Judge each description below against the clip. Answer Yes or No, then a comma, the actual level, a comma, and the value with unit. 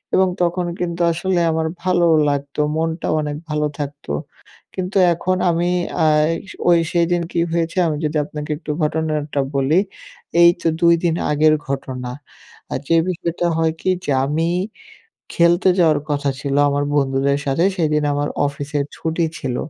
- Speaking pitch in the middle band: Yes, medium, 160 Hz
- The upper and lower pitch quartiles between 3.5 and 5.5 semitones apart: No, average, 2.9 semitones